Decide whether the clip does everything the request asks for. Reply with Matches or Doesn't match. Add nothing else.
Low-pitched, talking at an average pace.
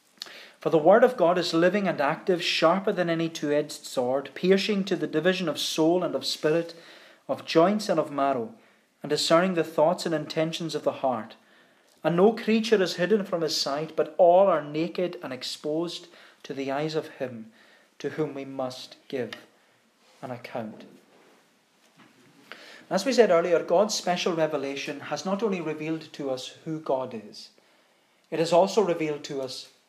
Doesn't match